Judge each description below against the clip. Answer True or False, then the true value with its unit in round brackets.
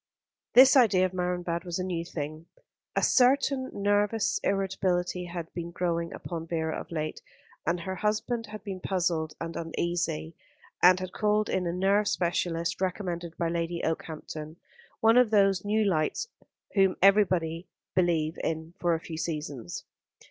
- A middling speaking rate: True (150 wpm)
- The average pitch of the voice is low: False (175 Hz)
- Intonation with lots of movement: False (3.0 semitones)